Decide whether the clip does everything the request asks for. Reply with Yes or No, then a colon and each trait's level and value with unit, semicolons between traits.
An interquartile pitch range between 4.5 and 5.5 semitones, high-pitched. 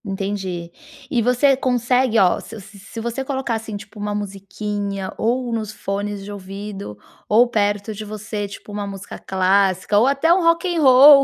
No: average, 3.7 semitones; high, 210 Hz